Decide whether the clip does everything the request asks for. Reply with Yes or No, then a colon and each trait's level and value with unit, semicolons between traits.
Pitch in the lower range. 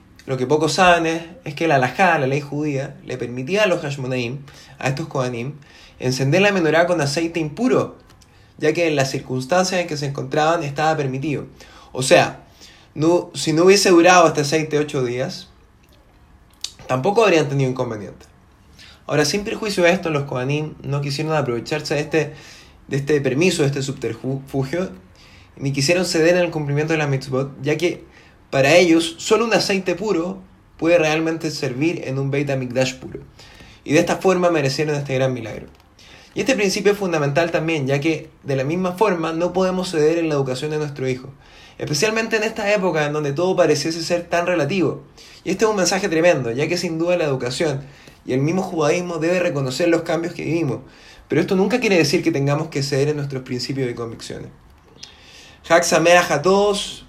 No: medium, 155 Hz